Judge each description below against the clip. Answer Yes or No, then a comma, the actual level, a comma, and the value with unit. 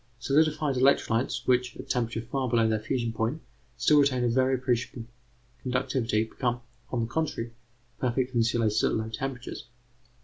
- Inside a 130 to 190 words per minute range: Yes, average, 145 wpm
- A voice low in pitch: Yes, low, 125 Hz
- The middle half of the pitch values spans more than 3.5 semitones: No, narrow, 2.5 semitones